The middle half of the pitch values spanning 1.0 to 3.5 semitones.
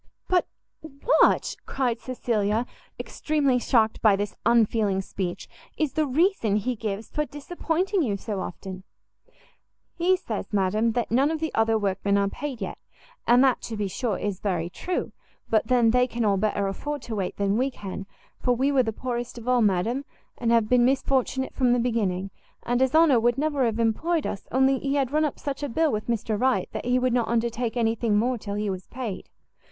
No: average, 4.1 semitones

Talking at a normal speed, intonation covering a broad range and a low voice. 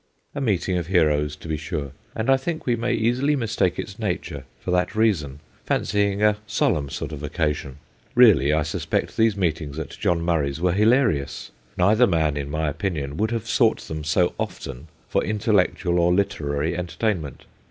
Yes: average, 175 wpm; wide, 6.2 semitones; very low, 90 Hz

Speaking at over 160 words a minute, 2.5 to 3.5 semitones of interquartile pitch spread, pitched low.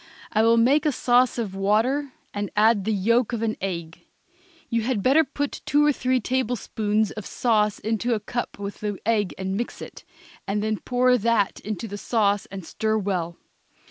No: average, 190 wpm; average, 3.2 semitones; high, 220 Hz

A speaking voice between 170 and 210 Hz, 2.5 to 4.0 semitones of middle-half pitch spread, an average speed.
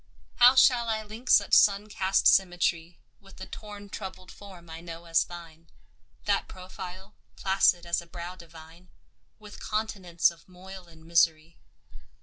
Yes: medium, 185 Hz; average, 3.0 semitones; average, 145 wpm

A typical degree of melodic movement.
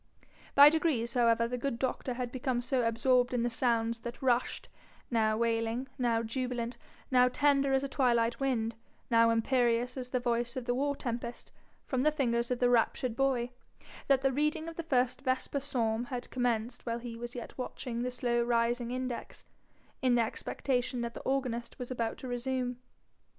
No: narrow, 1.8 semitones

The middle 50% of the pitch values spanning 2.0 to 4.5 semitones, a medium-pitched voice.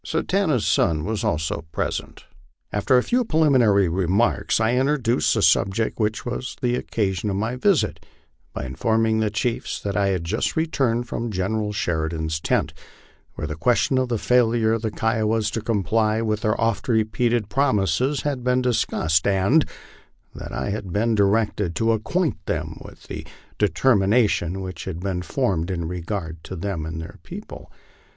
No: average, 4.1 semitones; low, 110 Hz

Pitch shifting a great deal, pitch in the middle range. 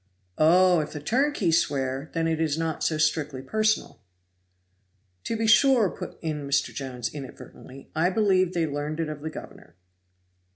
No: average, 4.1 semitones; medium, 160 Hz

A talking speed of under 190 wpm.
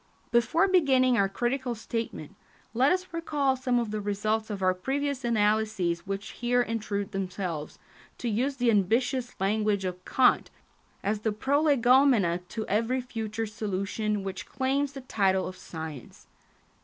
Yes: average, 145 wpm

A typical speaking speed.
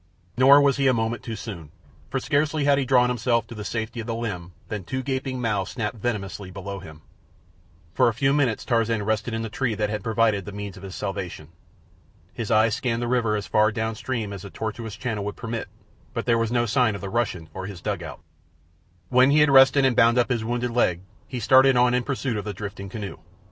No: fast, 225 wpm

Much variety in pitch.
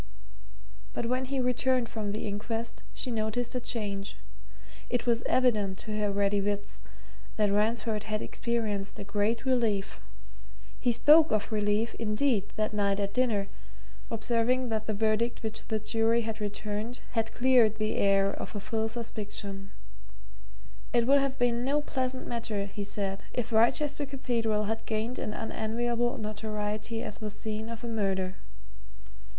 No: narrow, 2.4 semitones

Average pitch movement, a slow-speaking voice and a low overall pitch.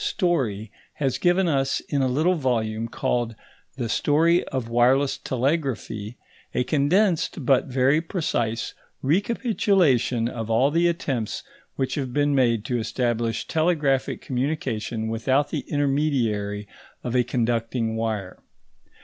Yes: average, 4.5 semitones; slow, 125 wpm; low, 130 Hz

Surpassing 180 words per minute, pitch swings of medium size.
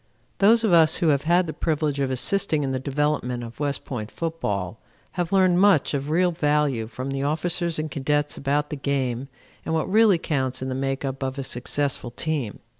Yes: average, 200 wpm; average, 3.7 semitones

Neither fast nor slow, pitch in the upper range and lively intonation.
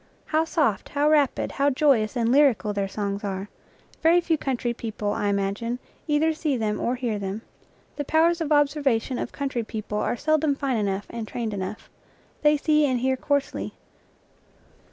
Yes: average, 170 wpm; very high, 255 Hz; wide, 5.7 semitones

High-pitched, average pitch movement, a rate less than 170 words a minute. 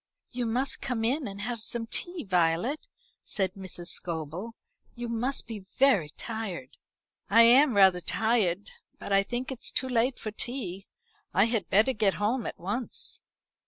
Yes: high, 225 Hz; average, 4.1 semitones; average, 160 wpm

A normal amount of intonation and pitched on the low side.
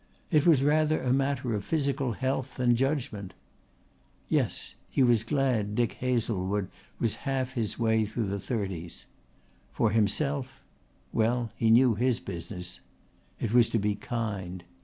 Yes: average, 4.2 semitones; low, 115 Hz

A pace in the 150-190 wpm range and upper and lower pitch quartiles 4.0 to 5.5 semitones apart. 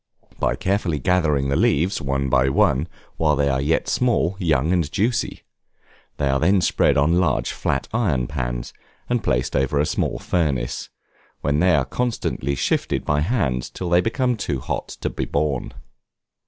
Yes: average, 170 wpm; average, 5.1 semitones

